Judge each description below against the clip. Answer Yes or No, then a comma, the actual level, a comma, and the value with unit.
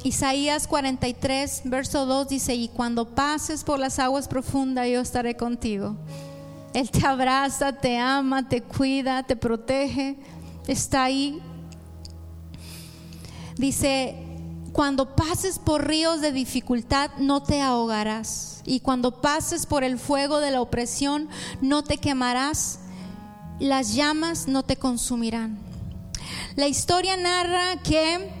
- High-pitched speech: Yes, very high, 265 Hz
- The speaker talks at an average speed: No, slow, 120 wpm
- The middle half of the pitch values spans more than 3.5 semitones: No, average, 3.2 semitones